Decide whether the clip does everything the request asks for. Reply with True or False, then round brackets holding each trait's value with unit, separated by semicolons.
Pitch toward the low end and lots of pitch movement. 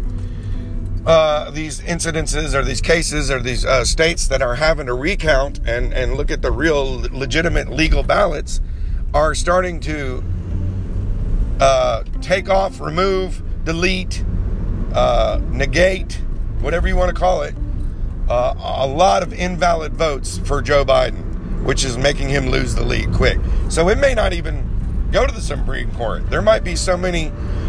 True (130 Hz; 8.4 semitones)